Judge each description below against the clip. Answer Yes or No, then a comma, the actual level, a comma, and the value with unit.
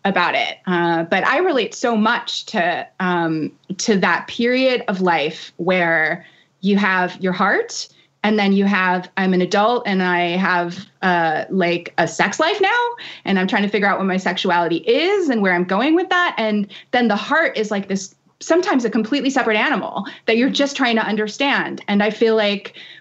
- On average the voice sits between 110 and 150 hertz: No, high, 205 Hz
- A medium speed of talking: Yes, average, 195 wpm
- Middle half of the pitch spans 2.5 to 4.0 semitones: No, average, 5.0 semitones